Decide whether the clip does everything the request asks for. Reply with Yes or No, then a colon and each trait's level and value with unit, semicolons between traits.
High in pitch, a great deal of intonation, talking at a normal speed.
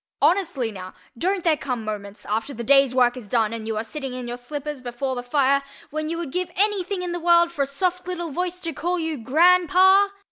No: very high, 290 Hz; wide, 6.2 semitones; fast, 235 wpm